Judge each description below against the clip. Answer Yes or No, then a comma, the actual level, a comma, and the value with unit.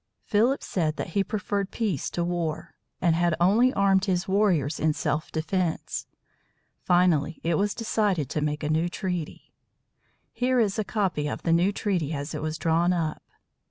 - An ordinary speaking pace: Yes, average, 170 wpm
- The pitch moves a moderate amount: Yes, average, 4.0 semitones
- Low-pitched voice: No, medium, 175 Hz